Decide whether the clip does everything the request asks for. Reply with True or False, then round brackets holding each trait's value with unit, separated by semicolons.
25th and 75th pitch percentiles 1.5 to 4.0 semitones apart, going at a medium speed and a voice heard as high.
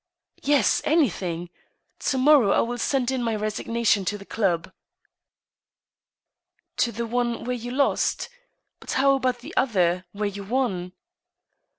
False (4.5 semitones; 150 wpm; 235 Hz)